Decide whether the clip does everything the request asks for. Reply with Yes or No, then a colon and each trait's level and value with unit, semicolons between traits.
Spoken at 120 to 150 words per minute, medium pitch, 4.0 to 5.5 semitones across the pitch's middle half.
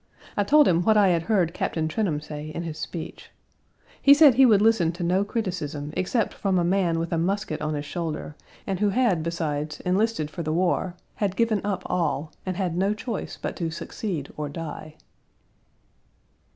No: average, 190 wpm; medium, 175 Hz; average, 4.5 semitones